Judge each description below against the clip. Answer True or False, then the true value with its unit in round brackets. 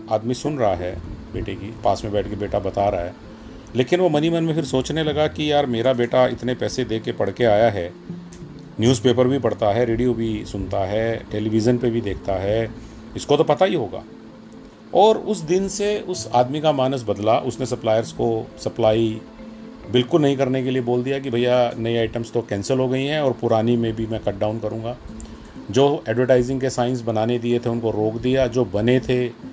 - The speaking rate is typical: False (205 wpm)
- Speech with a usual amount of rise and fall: True (3.3 semitones)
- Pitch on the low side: True (120 Hz)